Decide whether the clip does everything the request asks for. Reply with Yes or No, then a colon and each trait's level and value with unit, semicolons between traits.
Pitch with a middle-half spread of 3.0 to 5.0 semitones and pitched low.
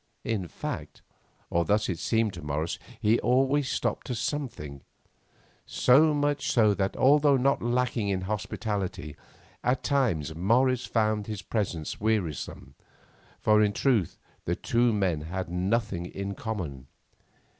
No: wide, 5.4 semitones; low, 105 Hz